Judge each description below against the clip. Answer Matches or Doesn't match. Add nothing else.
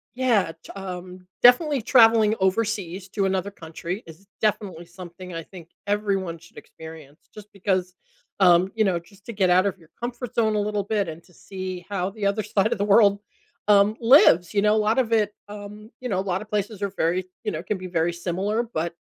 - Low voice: Doesn't match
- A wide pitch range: Doesn't match